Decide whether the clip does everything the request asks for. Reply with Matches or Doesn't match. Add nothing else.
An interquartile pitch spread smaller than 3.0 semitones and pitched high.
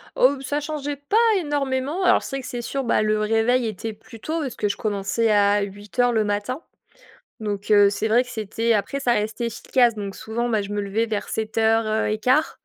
Doesn't match